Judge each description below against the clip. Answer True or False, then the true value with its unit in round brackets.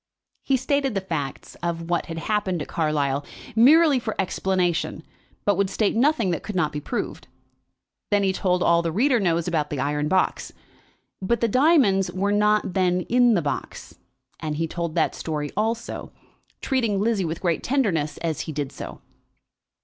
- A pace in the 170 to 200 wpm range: True (175 wpm)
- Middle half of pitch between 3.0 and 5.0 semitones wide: False (5.4 semitones)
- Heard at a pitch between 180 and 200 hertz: True (185 Hz)